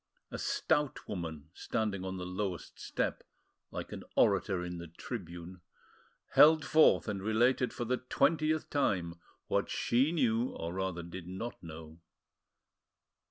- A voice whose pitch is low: Yes, very low, 95 Hz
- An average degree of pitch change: No, wide, 6.5 semitones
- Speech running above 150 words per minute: No, slow, 135 wpm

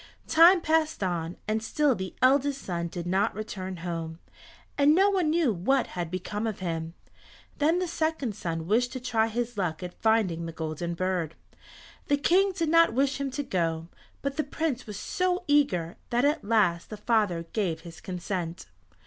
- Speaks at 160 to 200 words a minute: Yes, average, 180 wpm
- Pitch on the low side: No, high, 215 Hz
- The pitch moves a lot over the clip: Yes, wide, 8.6 semitones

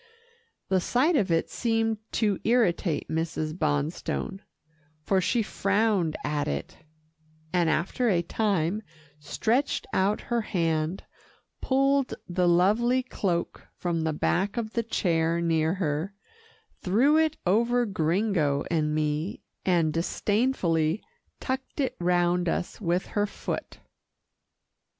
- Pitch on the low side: No, medium, 185 Hz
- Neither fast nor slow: No, slow, 120 wpm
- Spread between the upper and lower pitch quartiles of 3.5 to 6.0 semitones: Yes, wide, 5.4 semitones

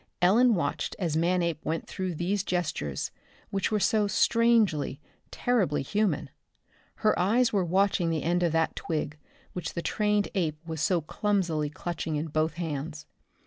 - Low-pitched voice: No, medium, 175 Hz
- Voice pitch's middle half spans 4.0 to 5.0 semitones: Yes, average, 4.4 semitones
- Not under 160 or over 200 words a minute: No, average, 150 wpm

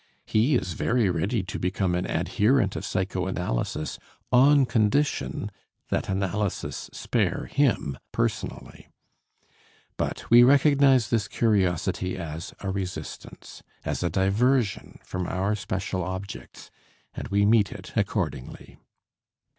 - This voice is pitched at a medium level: No, low, 100 Hz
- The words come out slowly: Yes, slow, 115 wpm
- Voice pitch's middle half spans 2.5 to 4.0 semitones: No, average, 4.5 semitones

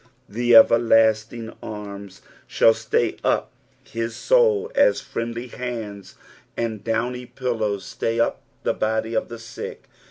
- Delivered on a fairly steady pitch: Yes, narrow, 1.6 semitones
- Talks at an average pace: No, slow, 125 wpm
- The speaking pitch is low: Yes, low, 115 Hz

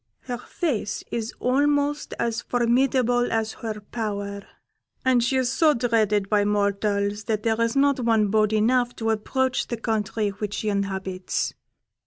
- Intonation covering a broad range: No, average, 3.0 semitones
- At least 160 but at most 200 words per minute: No, average, 150 wpm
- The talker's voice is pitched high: Yes, high, 225 Hz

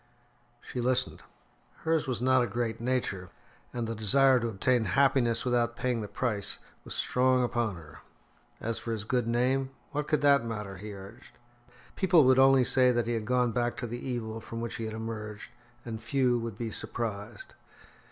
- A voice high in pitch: No, low, 120 Hz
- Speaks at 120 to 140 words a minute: No, average, 180 wpm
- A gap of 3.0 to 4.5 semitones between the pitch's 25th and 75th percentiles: No, narrow, 2.4 semitones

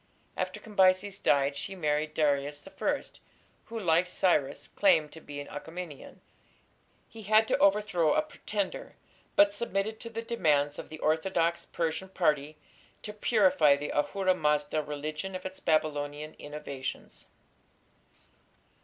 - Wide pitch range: No, average, 4.8 semitones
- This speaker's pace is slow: Yes, slow, 130 wpm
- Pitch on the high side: No, medium, 165 Hz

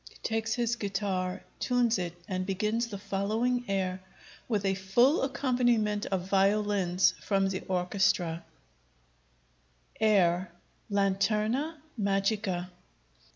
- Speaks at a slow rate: Yes, slow, 105 wpm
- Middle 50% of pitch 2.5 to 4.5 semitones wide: Yes, average, 2.8 semitones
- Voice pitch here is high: Yes, high, 200 Hz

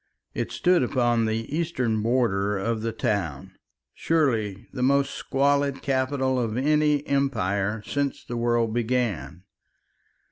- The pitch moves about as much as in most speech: Yes, average, 4.2 semitones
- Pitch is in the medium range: No, low, 120 Hz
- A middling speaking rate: No, slow, 120 wpm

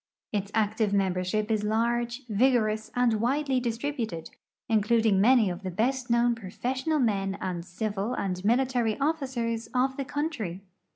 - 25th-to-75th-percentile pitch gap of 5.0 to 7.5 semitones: No, average, 3.8 semitones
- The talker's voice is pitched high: Yes, high, 225 Hz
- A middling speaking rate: Yes, average, 150 wpm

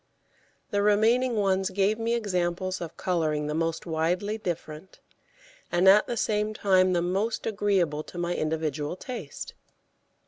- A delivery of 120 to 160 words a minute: Yes, average, 140 wpm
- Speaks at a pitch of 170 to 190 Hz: Yes, medium, 185 Hz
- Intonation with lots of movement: No, average, 4.0 semitones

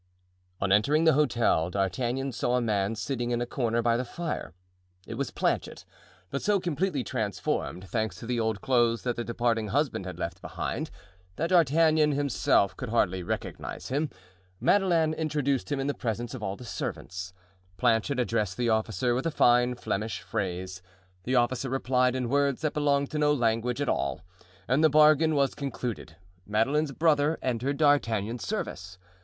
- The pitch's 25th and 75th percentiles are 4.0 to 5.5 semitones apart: Yes, average, 4.4 semitones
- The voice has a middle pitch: No, low, 125 Hz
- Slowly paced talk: No, average, 165 wpm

